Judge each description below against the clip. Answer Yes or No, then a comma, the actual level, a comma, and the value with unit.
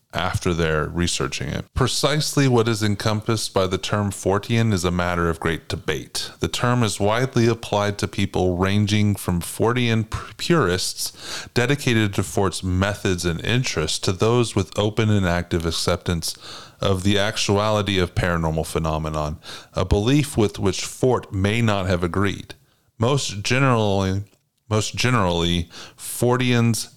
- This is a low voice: Yes, low, 105 Hz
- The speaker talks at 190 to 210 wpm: No, average, 140 wpm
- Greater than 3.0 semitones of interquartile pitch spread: Yes, average, 4.1 semitones